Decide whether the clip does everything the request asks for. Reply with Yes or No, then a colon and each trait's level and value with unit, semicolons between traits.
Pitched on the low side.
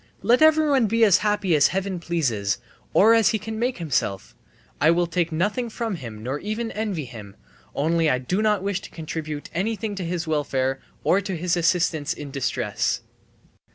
No: medium, 175 Hz